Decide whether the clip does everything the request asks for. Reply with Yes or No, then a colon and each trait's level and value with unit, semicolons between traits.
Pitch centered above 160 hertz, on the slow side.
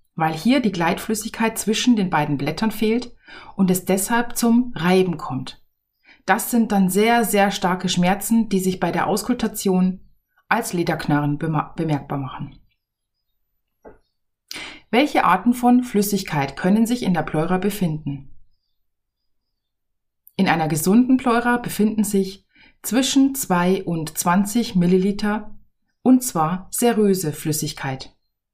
Yes: medium, 185 Hz; slow, 120 wpm